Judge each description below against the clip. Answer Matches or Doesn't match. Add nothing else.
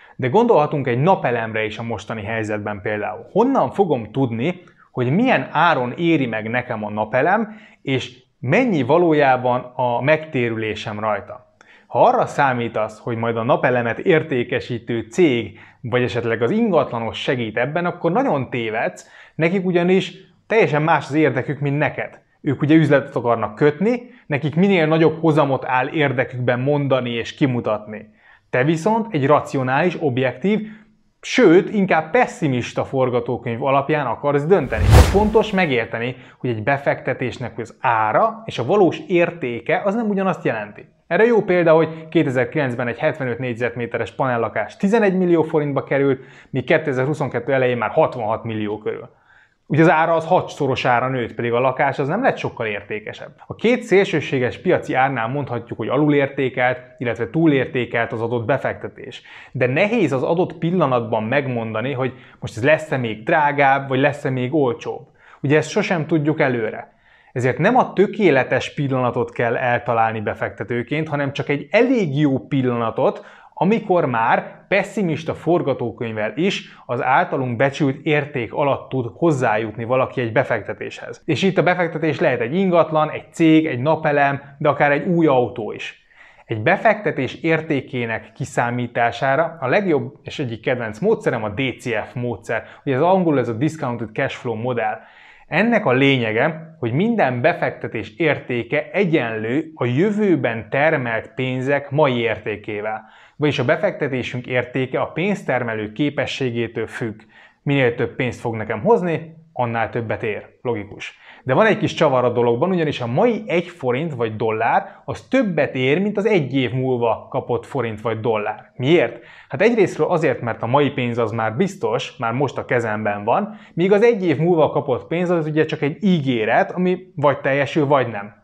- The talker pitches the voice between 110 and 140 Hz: Matches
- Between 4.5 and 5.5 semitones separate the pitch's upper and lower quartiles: Matches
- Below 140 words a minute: Doesn't match